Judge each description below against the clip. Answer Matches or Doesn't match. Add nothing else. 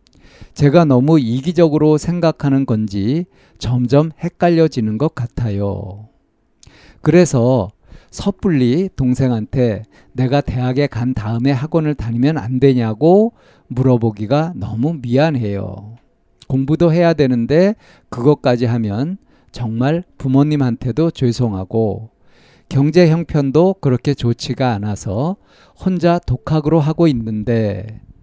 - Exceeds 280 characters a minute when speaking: Doesn't match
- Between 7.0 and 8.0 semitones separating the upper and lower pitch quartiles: Doesn't match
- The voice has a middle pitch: Doesn't match